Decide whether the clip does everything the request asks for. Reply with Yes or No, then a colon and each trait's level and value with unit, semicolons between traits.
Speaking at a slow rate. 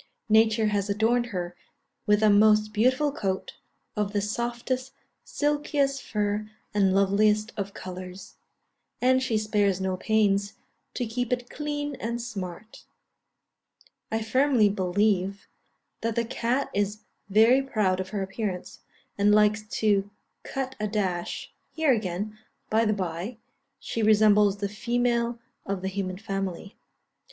Yes: slow, 130 wpm